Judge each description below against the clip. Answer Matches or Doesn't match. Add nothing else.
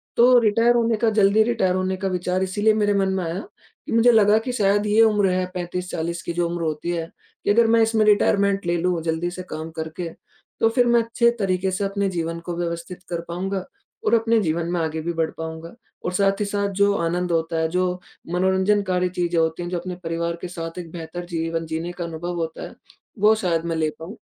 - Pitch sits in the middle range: Matches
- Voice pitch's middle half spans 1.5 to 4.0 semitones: Matches